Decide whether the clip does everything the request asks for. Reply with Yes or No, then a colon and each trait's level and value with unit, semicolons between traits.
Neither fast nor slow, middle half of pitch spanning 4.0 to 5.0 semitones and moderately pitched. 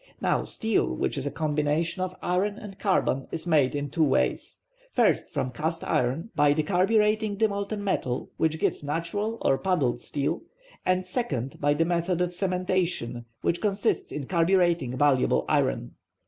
Yes: average, 160 wpm; average, 4.7 semitones; medium, 170 Hz